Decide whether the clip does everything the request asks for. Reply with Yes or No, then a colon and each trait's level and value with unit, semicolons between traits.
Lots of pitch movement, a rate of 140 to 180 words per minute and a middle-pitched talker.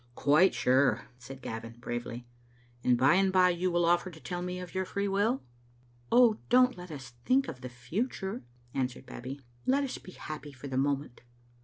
No: wide, 6.8 semitones; average, 190 wpm; medium, 170 Hz